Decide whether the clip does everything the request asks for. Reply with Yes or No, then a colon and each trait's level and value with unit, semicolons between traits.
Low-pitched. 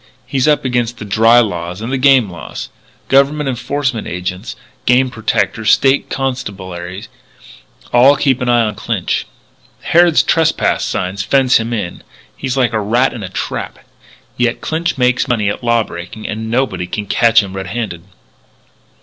Yes: low, 115 Hz